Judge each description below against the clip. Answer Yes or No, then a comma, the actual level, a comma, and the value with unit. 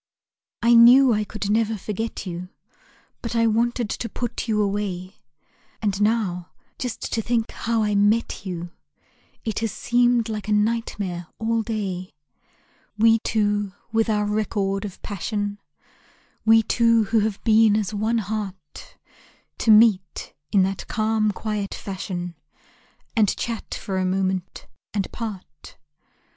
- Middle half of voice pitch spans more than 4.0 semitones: No, narrow, 2.5 semitones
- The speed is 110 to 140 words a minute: Yes, slow, 135 wpm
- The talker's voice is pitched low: No, high, 215 Hz